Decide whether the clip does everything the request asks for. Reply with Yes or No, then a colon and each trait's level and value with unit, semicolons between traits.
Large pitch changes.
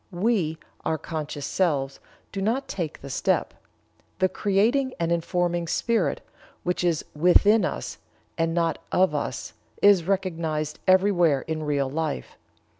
No: average, 3.8 semitones